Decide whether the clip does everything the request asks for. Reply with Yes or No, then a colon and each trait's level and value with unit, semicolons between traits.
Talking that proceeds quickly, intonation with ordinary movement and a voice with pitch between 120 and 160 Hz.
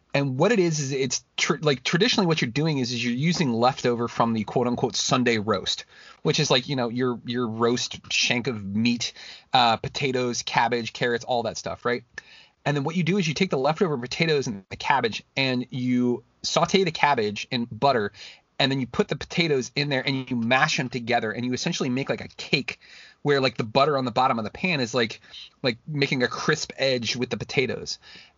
Yes: fast, 220 wpm; average, 3.1 semitones; low, 130 Hz